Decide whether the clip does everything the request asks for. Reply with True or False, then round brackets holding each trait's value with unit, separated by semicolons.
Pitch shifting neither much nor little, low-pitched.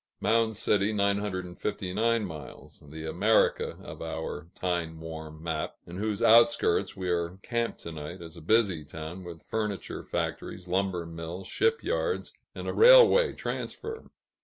True (4.9 semitones; 90 Hz)